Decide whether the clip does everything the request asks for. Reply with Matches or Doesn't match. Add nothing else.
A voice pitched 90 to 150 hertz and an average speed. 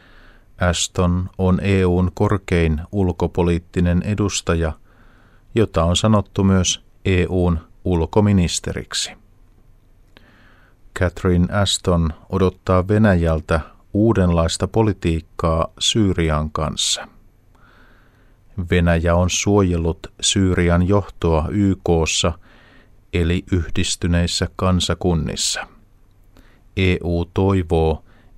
Doesn't match